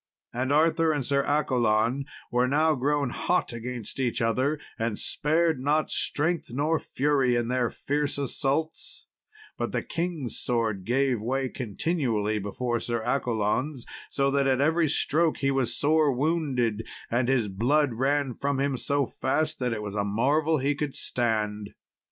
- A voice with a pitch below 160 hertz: Yes, low, 135 Hz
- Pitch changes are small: No, average, 3.8 semitones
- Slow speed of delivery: No, average, 155 wpm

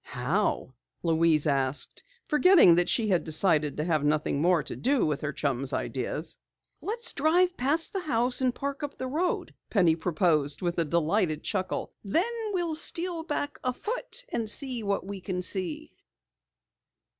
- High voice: Yes, high, 200 Hz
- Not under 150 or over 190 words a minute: Yes, average, 155 wpm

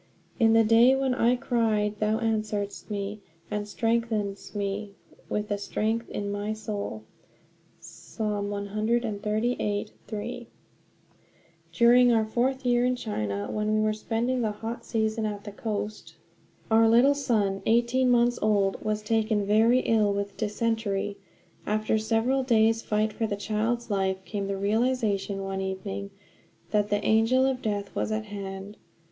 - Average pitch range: No, narrow, 2.2 semitones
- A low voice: No, high, 215 Hz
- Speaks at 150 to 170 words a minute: No, average, 140 wpm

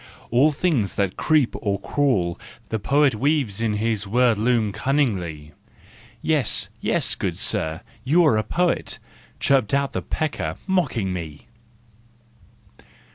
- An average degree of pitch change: No, wide, 6.4 semitones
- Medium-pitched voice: No, low, 120 Hz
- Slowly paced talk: Yes, slow, 130 wpm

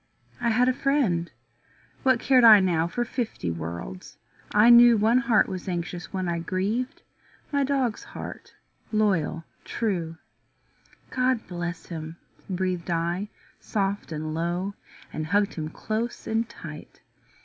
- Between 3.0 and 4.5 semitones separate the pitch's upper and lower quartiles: No, wide, 5.6 semitones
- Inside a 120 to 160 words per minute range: Yes, slow, 135 wpm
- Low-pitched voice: No, high, 195 Hz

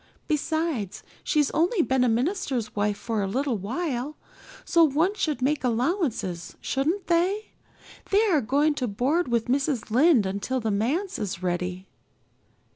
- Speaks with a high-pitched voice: Yes, very high, 265 Hz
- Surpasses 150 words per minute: No, average, 145 wpm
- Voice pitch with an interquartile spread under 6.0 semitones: No, wide, 6.8 semitones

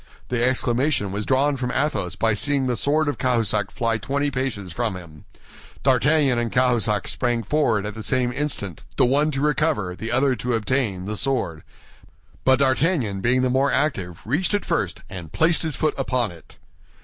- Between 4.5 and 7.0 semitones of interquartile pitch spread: Yes, average, 4.9 semitones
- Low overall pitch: Yes, low, 125 Hz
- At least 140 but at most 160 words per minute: No, average, 180 wpm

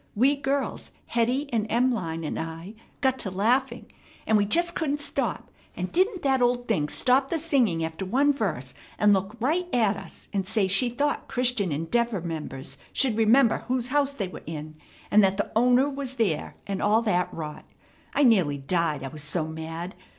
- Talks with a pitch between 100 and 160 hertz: No, high, 220 Hz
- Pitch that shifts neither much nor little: No, wide, 7.2 semitones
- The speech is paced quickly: No, average, 185 wpm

